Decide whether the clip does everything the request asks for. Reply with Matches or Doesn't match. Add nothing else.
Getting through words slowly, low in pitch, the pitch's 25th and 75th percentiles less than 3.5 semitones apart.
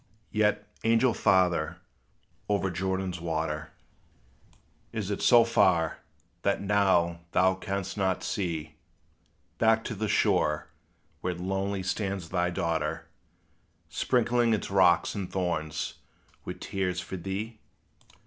Matches